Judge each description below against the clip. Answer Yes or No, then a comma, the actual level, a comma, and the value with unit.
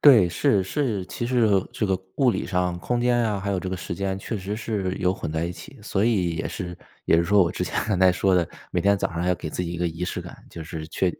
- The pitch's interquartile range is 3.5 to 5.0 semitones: No, average, 2.8 semitones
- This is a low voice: Yes, very low, 95 Hz